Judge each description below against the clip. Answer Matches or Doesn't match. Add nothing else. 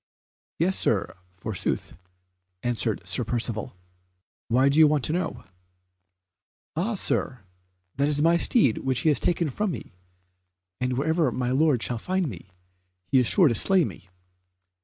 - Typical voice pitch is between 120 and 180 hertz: Matches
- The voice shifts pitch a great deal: Matches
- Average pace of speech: Matches